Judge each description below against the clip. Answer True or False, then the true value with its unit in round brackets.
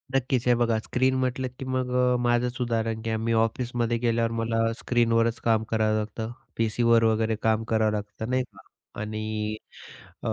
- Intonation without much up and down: True (1.8 semitones)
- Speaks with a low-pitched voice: True (115 Hz)